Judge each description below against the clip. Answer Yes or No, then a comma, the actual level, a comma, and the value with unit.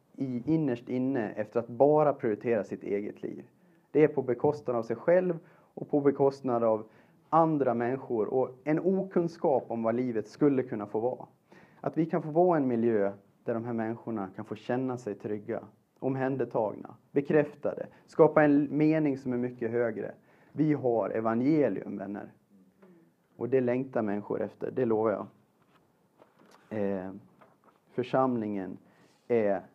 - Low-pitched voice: Yes, low, 125 Hz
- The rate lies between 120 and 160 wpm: Yes, average, 145 wpm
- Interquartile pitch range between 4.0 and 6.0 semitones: Yes, average, 4.5 semitones